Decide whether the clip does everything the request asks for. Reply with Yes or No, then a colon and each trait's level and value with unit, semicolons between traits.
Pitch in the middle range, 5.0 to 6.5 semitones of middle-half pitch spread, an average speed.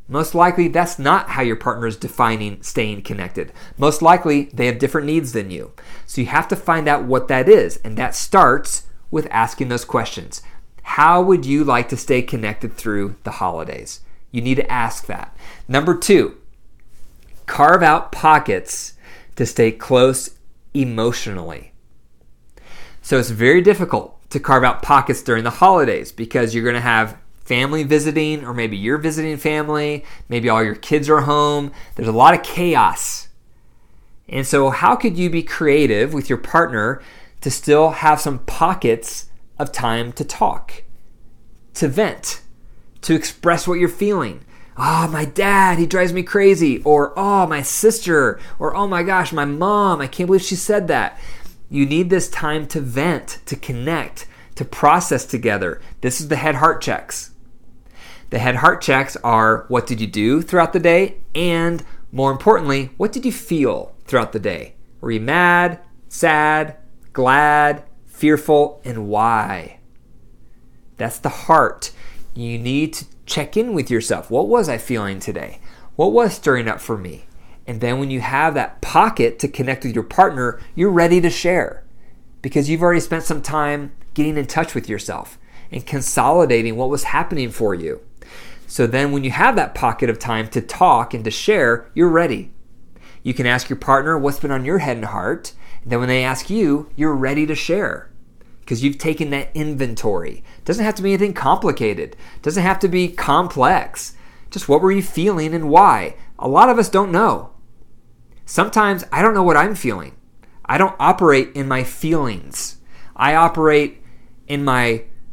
Yes: medium, 145 Hz; wide, 5.6 semitones; average, 170 wpm